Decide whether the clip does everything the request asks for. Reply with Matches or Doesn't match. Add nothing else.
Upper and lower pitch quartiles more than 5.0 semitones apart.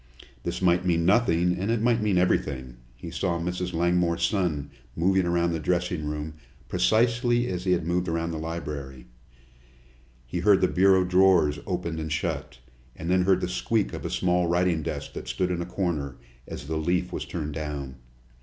Doesn't match